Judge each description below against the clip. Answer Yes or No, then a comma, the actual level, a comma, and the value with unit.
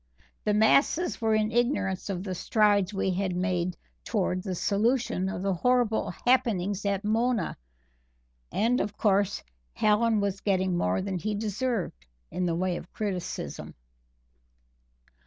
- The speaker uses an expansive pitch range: No, average, 3.0 semitones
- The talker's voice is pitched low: No, high, 200 Hz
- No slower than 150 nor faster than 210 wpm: No, average, 140 wpm